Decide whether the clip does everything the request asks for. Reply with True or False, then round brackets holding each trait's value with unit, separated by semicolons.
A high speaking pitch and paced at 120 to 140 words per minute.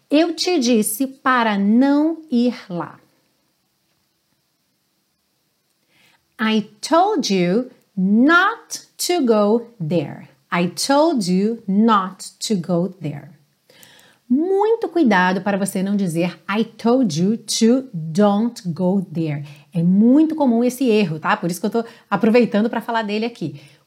True (220 Hz; 125 wpm)